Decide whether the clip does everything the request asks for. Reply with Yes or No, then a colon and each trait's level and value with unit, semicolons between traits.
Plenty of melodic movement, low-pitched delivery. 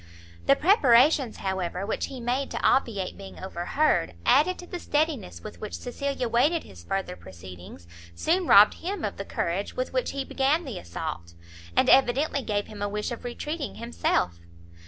No: wide, 8.0 semitones; high, 240 Hz